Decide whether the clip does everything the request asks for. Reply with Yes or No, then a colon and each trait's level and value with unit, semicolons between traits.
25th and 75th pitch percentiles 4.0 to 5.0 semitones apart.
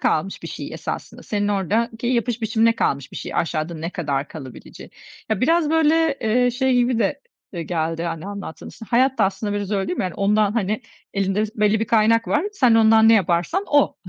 Yes: average, 4.4 semitones